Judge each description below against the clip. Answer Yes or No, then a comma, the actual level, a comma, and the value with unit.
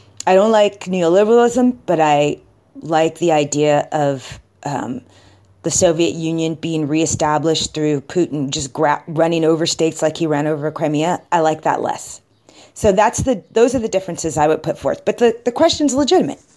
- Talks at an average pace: Yes, average, 175 wpm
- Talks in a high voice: No, medium, 160 Hz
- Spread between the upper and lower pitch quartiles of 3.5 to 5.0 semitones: Yes, average, 3.9 semitones